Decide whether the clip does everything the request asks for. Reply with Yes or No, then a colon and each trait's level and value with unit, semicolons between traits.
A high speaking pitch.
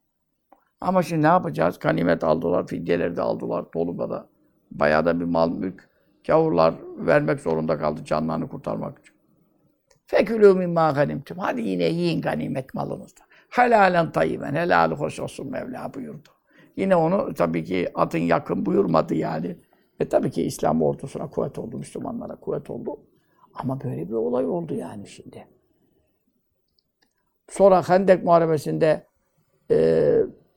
No: medium, 145 Hz